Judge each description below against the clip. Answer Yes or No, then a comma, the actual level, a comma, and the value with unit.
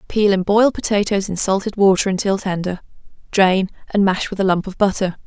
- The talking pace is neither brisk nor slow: Yes, average, 195 wpm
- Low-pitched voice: No, high, 195 Hz